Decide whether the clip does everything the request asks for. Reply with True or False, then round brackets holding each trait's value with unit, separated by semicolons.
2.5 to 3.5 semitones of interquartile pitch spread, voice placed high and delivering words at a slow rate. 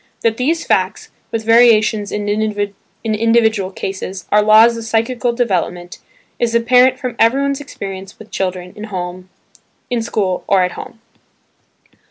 True (2.9 semitones; 220 Hz; 125 wpm)